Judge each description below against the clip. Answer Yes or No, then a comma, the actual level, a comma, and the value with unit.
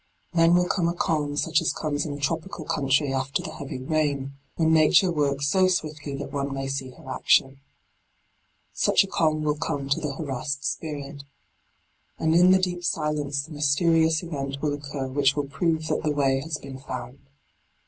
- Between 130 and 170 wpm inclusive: No, average, 185 wpm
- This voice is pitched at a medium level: Yes, medium, 145 Hz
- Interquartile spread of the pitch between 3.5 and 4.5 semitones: No, narrow, 2.5 semitones